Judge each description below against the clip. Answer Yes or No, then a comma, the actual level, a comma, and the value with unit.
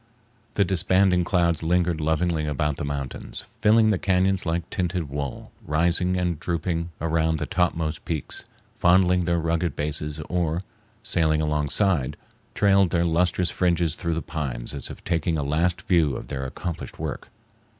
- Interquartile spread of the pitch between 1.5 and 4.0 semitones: Yes, narrow, 2.6 semitones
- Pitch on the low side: Yes, very low, 85 Hz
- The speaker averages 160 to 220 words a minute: No, average, 150 wpm